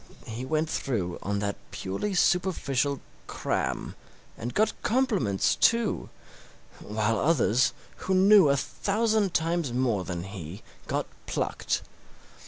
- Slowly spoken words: Yes, slow, 115 wpm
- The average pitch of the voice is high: No, low, 135 Hz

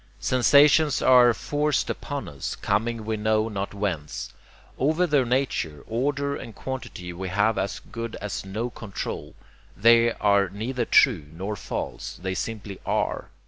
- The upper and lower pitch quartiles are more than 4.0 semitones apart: Yes, average, 4.6 semitones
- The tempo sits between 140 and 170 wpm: Yes, average, 145 wpm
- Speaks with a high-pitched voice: No, low, 110 Hz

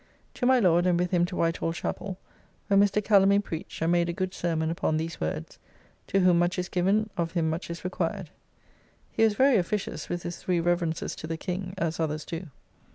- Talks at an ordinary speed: No, fast, 215 wpm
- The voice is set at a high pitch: No, medium, 175 Hz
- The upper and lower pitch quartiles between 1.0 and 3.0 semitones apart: Yes, narrow, 2.6 semitones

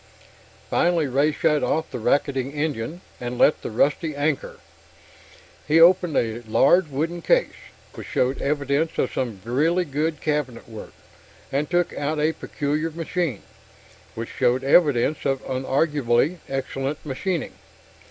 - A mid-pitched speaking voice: Yes, medium, 145 Hz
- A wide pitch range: No, average, 3.5 semitones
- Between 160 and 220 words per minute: No, slow, 135 wpm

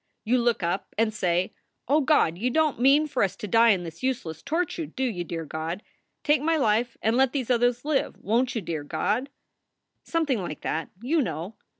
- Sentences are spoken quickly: Yes, fast, 210 wpm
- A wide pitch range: Yes, wide, 6.9 semitones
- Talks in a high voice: Yes, high, 235 Hz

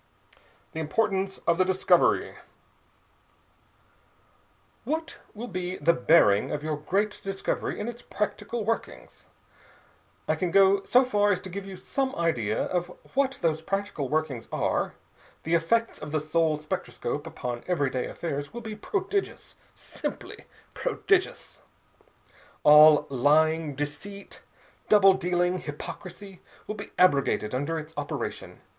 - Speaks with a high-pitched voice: No, medium, 175 Hz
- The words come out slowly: Yes, slow, 125 wpm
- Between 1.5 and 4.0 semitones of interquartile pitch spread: No, average, 5.2 semitones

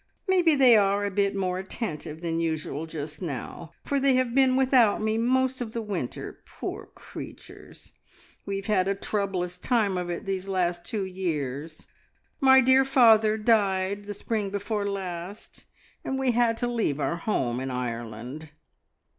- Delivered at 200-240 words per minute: No, average, 165 wpm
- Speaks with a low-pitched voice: No, high, 200 Hz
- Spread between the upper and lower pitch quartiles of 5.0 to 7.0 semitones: Yes, wide, 5.4 semitones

